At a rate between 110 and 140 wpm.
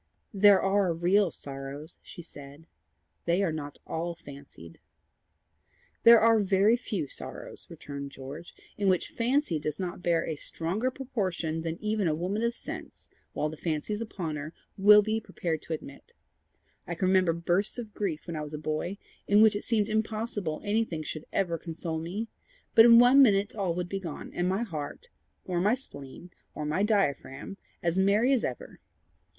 No: average, 175 wpm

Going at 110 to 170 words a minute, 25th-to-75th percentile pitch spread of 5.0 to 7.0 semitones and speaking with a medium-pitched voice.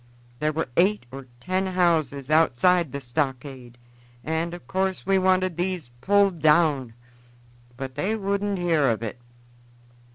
Yes: slow, 135 wpm; wide, 5.4 semitones; medium, 165 Hz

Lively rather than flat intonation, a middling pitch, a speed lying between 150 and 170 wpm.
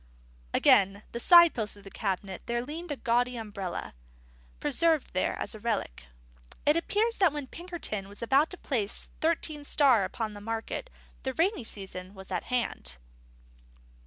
No: wide, 7.4 semitones; high, 235 Hz; average, 160 wpm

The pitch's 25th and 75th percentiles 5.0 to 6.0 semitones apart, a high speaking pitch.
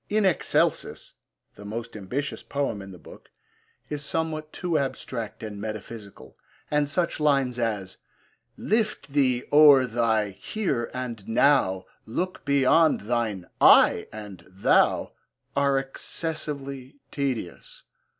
No: wide, 5.4 semitones; low, 130 Hz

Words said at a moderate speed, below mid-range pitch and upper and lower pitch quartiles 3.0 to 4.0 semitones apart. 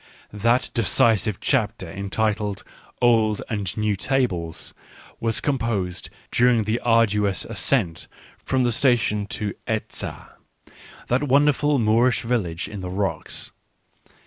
No: slow, 120 wpm; low, 110 Hz; average, 3.3 semitones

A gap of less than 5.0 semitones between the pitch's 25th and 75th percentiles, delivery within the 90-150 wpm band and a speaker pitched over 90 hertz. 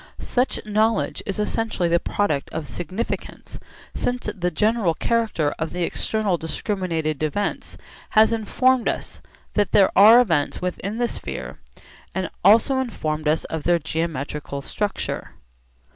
No: wide, 5.4 semitones; slow, 135 wpm; high, 190 Hz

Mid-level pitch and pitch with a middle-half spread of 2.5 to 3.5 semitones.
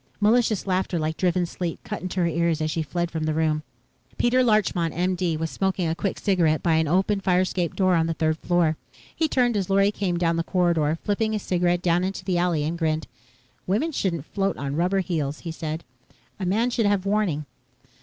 Yes: medium, 175 Hz; average, 3.2 semitones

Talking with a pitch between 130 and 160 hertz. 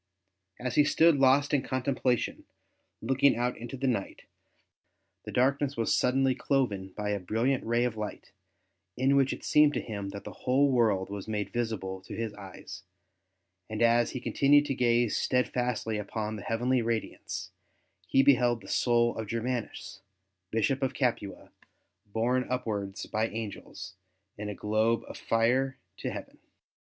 No: low, 120 Hz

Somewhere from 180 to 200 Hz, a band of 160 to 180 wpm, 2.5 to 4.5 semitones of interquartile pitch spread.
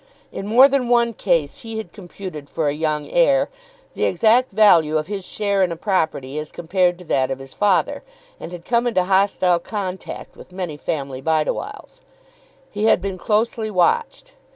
No: medium, 185 Hz; average, 175 wpm; wide, 5.4 semitones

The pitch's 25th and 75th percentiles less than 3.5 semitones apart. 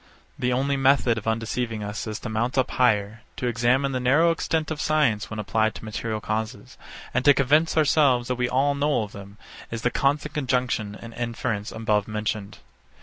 No: average, 3.9 semitones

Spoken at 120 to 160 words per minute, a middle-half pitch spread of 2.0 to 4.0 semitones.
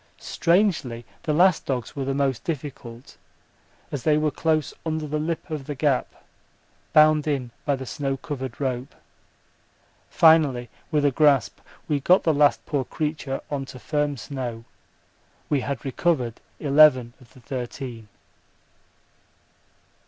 Yes: slow, 135 wpm; average, 3.0 semitones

